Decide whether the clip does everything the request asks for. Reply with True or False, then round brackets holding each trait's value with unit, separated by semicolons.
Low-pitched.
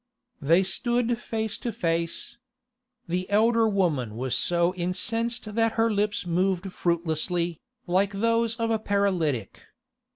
False (195 Hz)